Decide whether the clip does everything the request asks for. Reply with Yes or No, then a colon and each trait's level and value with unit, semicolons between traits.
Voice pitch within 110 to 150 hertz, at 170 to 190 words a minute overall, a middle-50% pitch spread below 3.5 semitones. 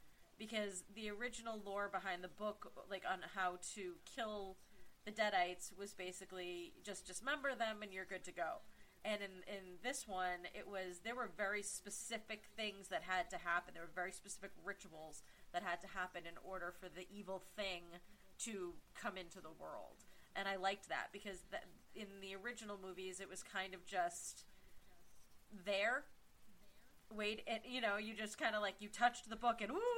No: high, 195 Hz; average, 185 wpm; narrow, 2.5 semitones